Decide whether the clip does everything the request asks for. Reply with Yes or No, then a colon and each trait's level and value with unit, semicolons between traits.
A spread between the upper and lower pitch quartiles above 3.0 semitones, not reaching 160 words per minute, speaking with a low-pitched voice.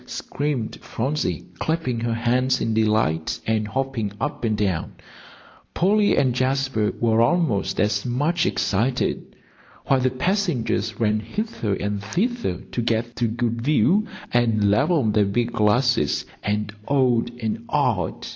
Yes: average, 3.9 semitones; average, 140 wpm; low, 120 Hz